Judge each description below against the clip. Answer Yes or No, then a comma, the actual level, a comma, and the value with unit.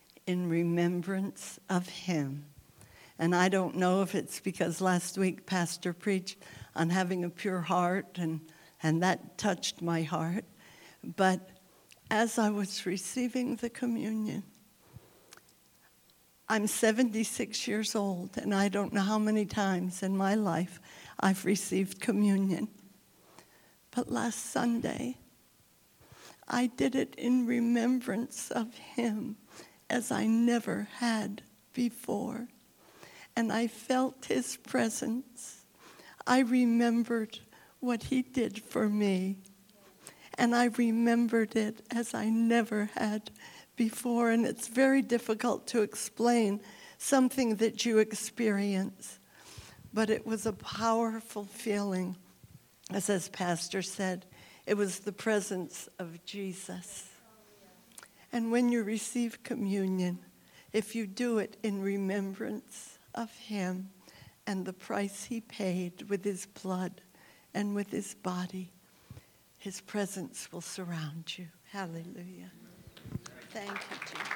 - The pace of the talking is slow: Yes, slow, 115 wpm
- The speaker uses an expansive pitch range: No, average, 3.8 semitones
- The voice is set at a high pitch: Yes, high, 205 Hz